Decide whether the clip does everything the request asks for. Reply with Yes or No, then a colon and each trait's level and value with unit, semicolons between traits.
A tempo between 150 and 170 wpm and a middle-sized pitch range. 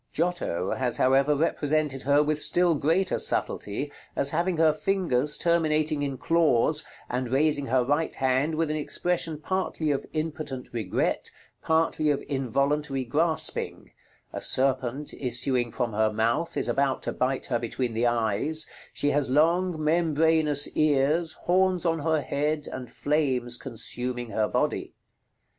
No: average, 140 wpm; average, 3.7 semitones